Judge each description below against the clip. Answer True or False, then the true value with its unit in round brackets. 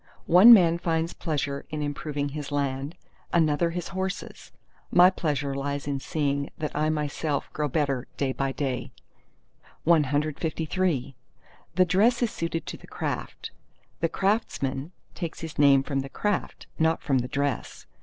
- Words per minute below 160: True (145 wpm)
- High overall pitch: False (150 Hz)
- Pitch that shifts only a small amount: False (3.1 semitones)